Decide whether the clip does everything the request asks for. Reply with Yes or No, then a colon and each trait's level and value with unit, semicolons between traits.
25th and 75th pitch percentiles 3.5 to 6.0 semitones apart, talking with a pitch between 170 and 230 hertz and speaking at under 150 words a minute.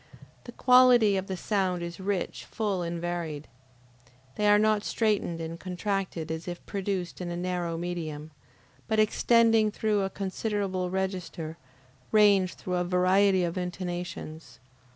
No: average, 2.9 semitones; medium, 185 Hz; average, 140 wpm